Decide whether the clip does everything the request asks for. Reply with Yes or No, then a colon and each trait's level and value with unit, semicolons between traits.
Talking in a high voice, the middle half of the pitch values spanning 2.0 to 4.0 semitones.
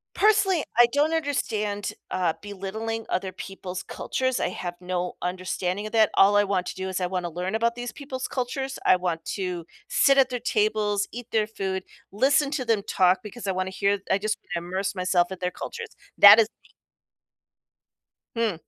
No: high, 205 Hz; average, 4.5 semitones